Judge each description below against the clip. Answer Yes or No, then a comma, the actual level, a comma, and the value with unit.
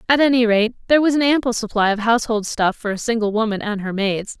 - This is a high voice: Yes, high, 225 Hz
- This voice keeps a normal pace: No, fast, 245 wpm